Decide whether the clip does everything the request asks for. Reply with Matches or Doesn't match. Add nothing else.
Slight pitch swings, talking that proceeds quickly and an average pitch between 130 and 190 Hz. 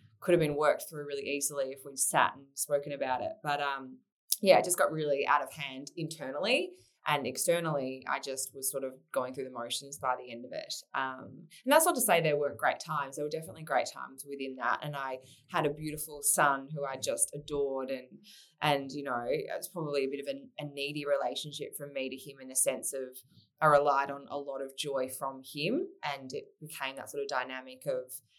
Matches